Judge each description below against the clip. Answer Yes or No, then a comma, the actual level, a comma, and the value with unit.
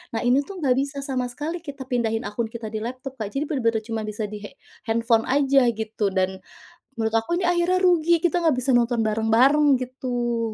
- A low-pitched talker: No, high, 245 Hz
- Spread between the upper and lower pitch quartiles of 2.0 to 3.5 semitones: No, average, 4.1 semitones